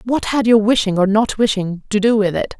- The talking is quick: Yes, fast, 255 wpm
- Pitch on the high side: Yes, high, 210 Hz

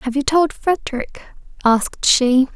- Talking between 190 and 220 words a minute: No, average, 140 wpm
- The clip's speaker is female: Yes, female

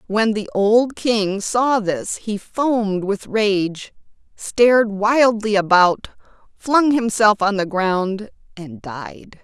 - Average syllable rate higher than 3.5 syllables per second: No, 3.1 syllables/s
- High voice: Yes, high, 210 Hz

